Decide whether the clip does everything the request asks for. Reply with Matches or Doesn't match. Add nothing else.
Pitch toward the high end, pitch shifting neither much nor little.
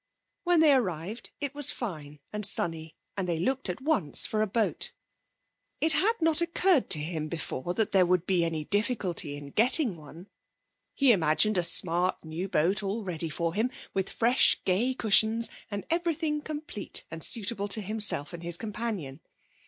Doesn't match